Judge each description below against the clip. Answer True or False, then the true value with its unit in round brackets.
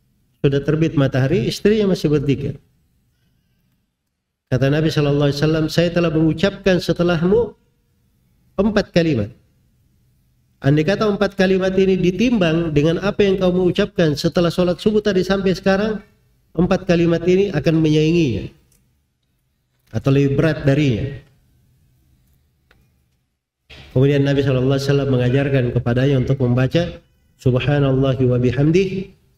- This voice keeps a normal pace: True (110 wpm)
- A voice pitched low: False (155 Hz)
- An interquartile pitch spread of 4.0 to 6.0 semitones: True (5.3 semitones)